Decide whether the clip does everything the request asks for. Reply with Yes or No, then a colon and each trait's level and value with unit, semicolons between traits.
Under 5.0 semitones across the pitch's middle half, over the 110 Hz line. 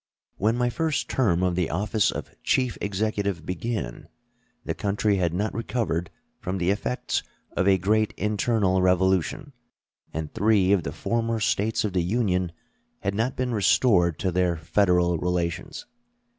No: average, 3.6 semitones; low, 100 Hz